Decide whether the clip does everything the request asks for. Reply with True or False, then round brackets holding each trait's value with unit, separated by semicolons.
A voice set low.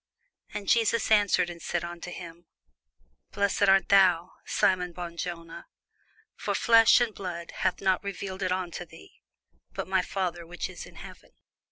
False (180 Hz)